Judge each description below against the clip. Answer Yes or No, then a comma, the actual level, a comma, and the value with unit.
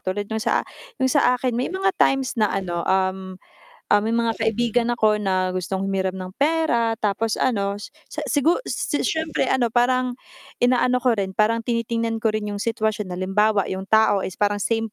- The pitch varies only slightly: No, average, 3.8 semitones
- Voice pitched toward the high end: Yes, high, 220 Hz